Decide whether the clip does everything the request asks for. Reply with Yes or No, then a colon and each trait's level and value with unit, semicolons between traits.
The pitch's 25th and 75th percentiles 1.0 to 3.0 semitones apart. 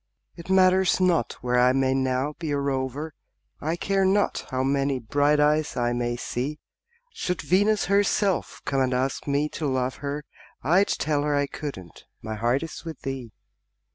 No: average, 4.2 semitones